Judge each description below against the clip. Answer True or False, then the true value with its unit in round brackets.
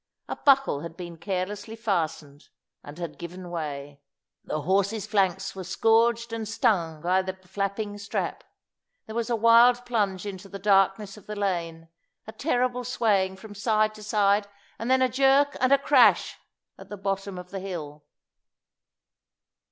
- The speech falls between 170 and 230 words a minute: False (160 wpm)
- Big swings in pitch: False (3.8 semitones)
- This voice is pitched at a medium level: False (200 Hz)